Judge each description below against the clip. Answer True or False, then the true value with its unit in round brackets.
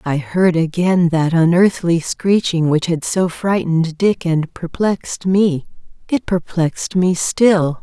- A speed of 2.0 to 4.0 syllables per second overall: True (3.8 syllables/s)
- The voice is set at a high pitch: False (175 Hz)